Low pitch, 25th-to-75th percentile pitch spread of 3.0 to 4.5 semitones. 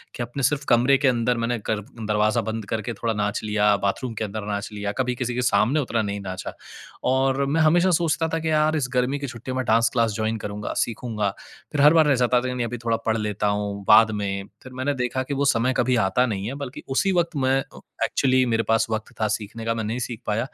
Yes: low, 120 Hz; average, 3.5 semitones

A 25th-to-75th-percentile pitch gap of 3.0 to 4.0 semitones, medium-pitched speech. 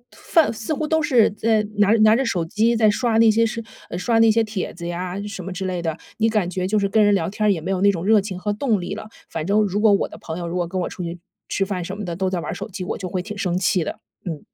No: average, 3.4 semitones; high, 200 Hz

